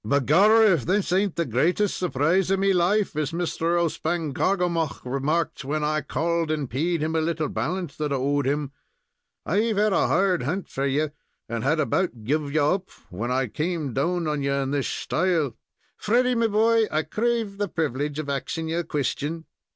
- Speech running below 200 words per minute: Yes, average, 185 wpm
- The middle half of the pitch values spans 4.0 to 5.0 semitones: Yes, average, 4.5 semitones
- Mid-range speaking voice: Yes, medium, 160 Hz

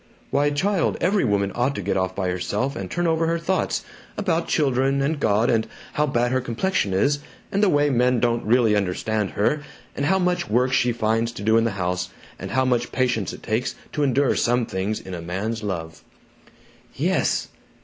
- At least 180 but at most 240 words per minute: Yes, average, 200 wpm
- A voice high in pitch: No, low, 120 Hz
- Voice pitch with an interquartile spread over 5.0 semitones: Yes, wide, 5.6 semitones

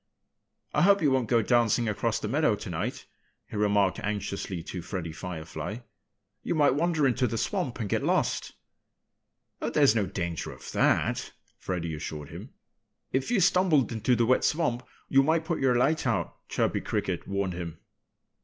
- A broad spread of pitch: Yes, wide, 6.7 semitones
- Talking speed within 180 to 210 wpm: No, average, 165 wpm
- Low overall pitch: Yes, low, 115 Hz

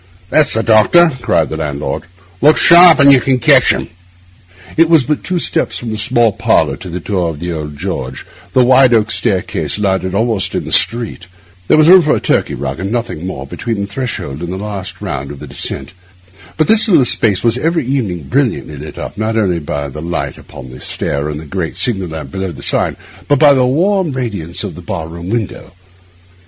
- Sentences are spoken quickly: Yes, fast, 215 wpm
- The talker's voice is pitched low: Yes, low, 105 Hz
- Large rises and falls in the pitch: Yes, wide, 7.8 semitones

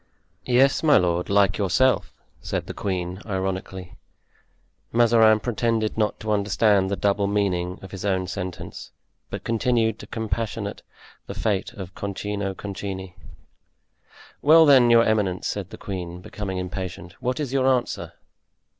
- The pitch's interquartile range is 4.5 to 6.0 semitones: No, average, 3.4 semitones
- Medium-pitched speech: No, low, 100 Hz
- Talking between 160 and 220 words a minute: No, slow, 135 wpm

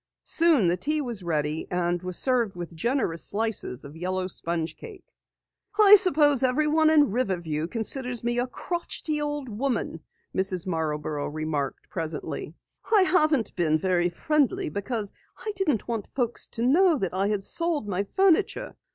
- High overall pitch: Yes, high, 225 Hz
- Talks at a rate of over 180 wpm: No, average, 150 wpm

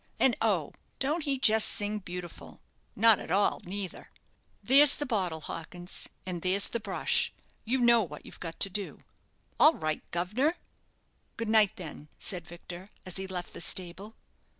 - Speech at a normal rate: Yes, average, 160 wpm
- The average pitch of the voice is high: Yes, high, 195 Hz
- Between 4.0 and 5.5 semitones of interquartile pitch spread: Yes, average, 4.3 semitones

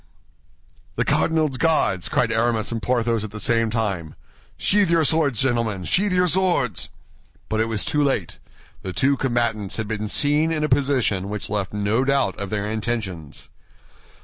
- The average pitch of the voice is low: Yes, low, 115 Hz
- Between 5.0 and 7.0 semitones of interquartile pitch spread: Yes, average, 5.3 semitones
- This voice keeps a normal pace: Yes, average, 165 wpm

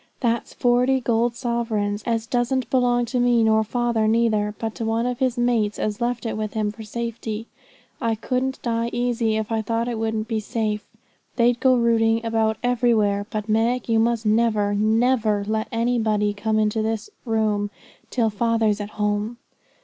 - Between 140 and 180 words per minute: Yes, average, 175 wpm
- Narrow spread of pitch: Yes, narrow, 1.8 semitones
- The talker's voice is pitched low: No, high, 225 Hz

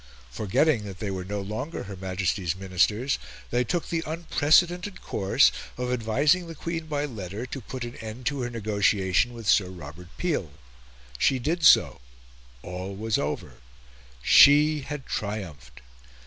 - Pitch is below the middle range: Yes, low, 110 Hz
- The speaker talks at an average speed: Yes, average, 150 wpm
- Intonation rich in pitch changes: Yes, wide, 7.2 semitones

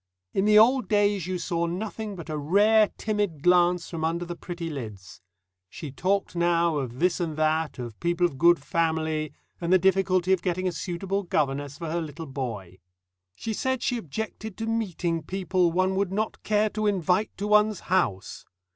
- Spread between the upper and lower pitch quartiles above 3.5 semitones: Yes, average, 4.1 semitones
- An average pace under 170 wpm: No, average, 180 wpm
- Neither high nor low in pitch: Yes, medium, 175 Hz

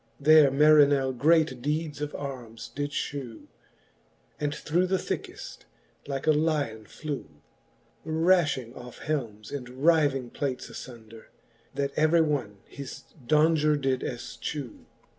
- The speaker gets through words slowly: Yes, slow, 120 wpm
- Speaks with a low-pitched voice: No, medium, 145 Hz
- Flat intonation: No, average, 3.3 semitones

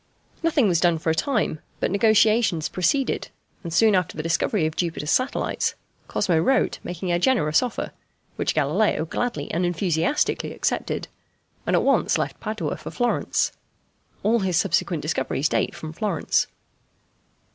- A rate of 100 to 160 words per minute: Yes, average, 145 wpm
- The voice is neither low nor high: Yes, medium, 180 Hz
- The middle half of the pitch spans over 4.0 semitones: Yes, wide, 5.5 semitones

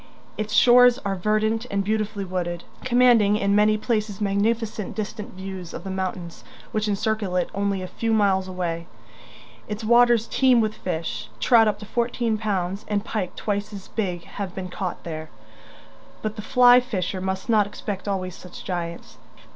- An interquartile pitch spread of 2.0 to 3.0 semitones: Yes, average, 2.7 semitones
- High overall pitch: Yes, high, 205 Hz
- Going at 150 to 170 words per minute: Yes, average, 165 wpm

